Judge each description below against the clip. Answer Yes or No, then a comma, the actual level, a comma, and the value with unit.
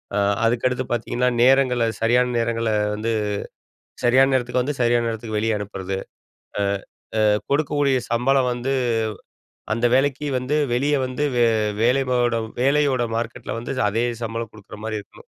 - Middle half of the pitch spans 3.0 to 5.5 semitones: No, narrow, 2.5 semitones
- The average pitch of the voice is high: No, low, 120 Hz